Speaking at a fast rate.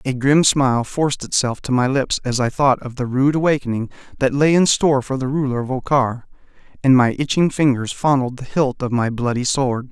Yes: fast, 210 wpm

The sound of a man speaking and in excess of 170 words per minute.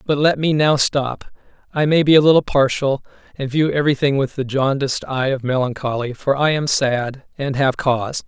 Yes: male; average, 180 wpm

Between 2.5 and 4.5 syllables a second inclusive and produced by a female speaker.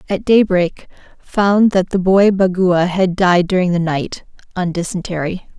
Yes: 4.2 syllables/s; female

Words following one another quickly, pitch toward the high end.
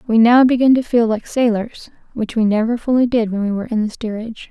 Yes: fast, 240 wpm; high, 230 Hz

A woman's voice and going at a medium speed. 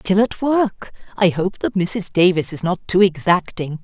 Yes: female; average, 190 wpm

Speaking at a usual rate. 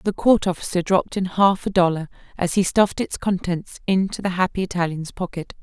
Yes: average, 190 wpm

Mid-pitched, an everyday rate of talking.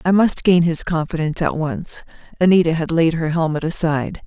Yes: medium, 165 Hz; average, 185 wpm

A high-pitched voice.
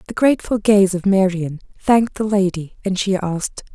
Yes: high, 195 Hz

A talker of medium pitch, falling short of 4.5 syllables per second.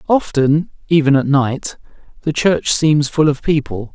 Yes: medium, 145 Hz; 4.2 syllables/s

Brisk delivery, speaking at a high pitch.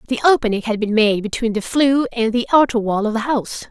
Yes: fast, 245 wpm; high, 230 Hz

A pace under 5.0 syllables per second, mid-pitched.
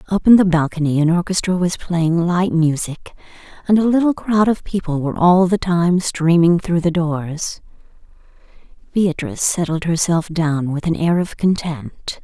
Yes: 4.6 syllables/s; medium, 170 Hz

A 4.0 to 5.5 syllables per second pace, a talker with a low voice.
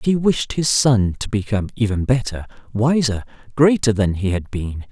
Yes: 5.0 syllables/s; low, 115 Hz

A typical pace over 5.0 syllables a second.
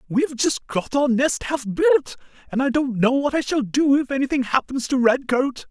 Yes: 5.2 syllables/s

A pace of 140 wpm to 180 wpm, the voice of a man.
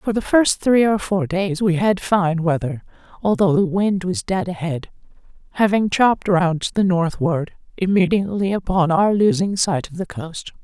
No: average, 175 wpm; female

